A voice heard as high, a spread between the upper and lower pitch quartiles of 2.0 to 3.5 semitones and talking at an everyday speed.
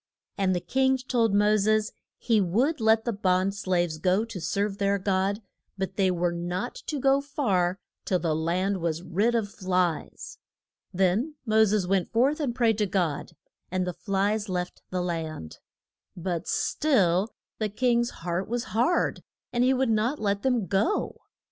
No: high, 200 Hz; average, 4.2 semitones; average, 165 wpm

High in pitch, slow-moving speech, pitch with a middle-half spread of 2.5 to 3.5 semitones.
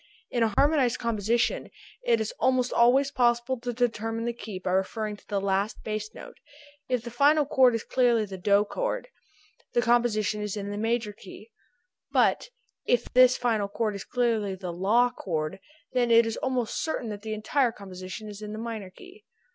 No: high, 230 Hz; average, 185 wpm; average, 3.0 semitones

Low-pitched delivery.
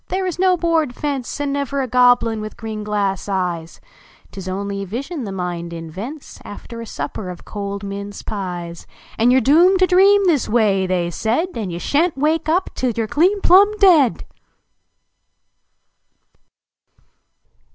No: high, 230 Hz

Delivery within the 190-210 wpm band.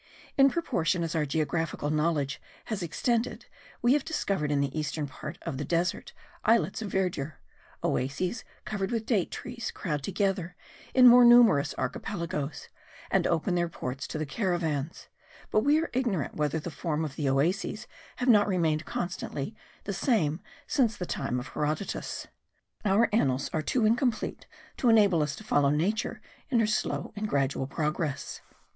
No: average, 160 wpm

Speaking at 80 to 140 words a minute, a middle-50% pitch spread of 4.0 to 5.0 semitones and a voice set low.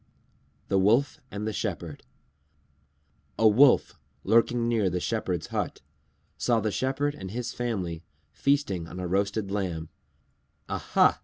Yes: slow, 135 wpm; average, 4.6 semitones; low, 105 Hz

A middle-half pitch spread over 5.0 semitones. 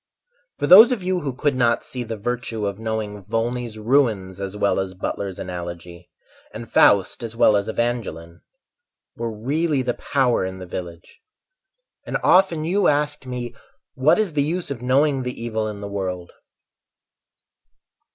Yes: wide, 5.5 semitones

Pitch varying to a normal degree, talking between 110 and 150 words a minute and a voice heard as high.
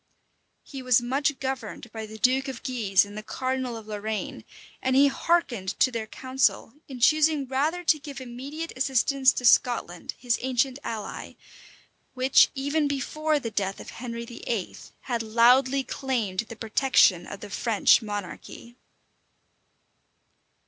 Yes: average, 3.4 semitones; average, 145 wpm; very high, 250 Hz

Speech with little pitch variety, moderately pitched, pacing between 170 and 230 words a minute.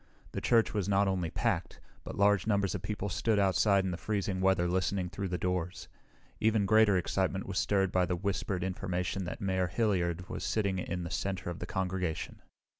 No: narrow, 1.8 semitones; very low, 95 Hz; average, 190 wpm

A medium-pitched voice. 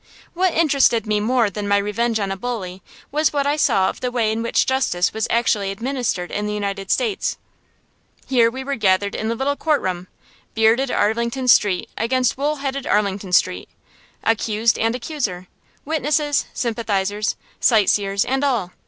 No: high, 230 Hz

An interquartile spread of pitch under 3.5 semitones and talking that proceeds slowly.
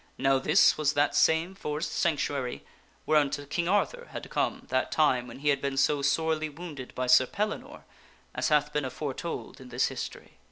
No: average, 2.9 semitones; average, 175 wpm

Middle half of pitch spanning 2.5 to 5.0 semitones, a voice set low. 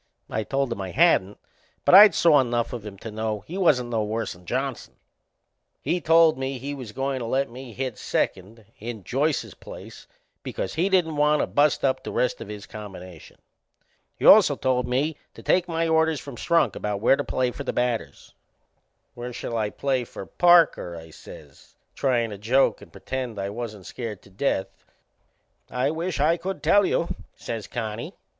No: wide, 5.5 semitones; low, 125 Hz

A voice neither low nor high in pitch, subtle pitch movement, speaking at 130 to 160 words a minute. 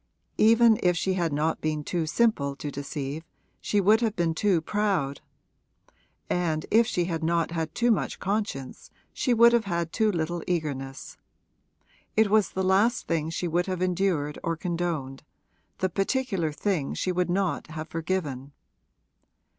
No: medium, 175 Hz; average, 4.2 semitones; average, 155 wpm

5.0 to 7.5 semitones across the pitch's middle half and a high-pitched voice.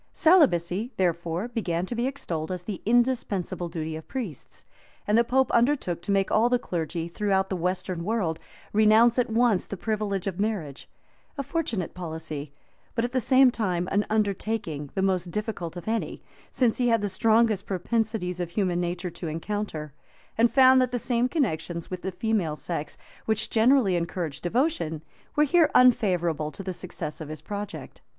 Yes: average, 5.3 semitones; high, 195 Hz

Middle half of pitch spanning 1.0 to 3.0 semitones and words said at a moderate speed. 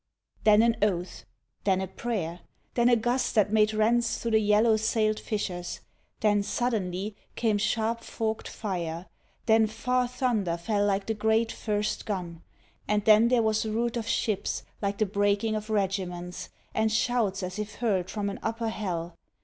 Yes: narrow, 2.4 semitones; average, 165 wpm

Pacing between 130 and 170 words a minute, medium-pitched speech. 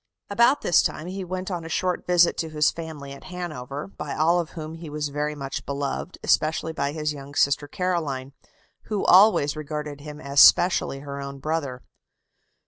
No: average, 180 wpm; medium, 155 Hz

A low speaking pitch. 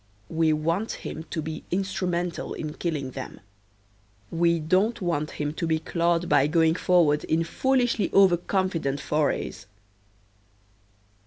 No: medium, 165 Hz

